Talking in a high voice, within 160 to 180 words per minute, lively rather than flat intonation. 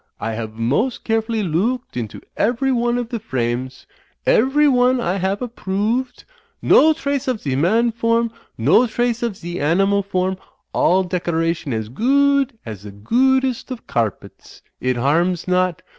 Yes: high, 200 Hz; average, 165 wpm; wide, 7.7 semitones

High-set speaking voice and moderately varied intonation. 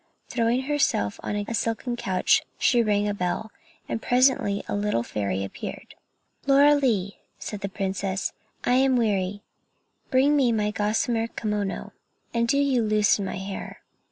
Yes: high, 215 Hz; average, 3.7 semitones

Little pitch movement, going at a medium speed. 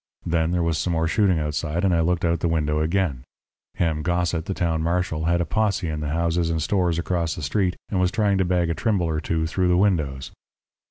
No: narrow, 2.1 semitones; fast, 230 wpm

